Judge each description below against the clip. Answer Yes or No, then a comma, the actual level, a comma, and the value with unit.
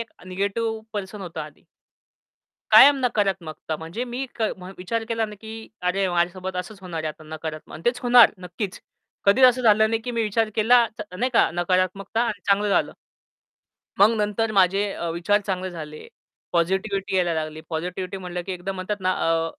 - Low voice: No, high, 195 Hz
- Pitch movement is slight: No, average, 3.7 semitones